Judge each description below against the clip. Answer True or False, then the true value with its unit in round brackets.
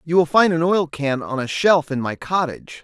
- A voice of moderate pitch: True (160 Hz)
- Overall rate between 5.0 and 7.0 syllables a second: True (5.1 syllables/s)